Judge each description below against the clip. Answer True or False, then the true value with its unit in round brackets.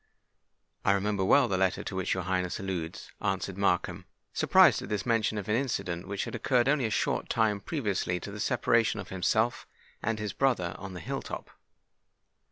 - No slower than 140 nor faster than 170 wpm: False (185 wpm)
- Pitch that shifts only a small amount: False (3.2 semitones)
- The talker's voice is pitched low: True (100 Hz)